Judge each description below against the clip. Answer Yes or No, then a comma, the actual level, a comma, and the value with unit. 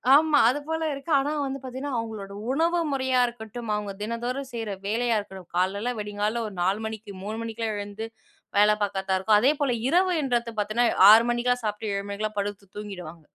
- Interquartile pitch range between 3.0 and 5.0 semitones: Yes, average, 3.6 semitones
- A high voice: Yes, high, 220 Hz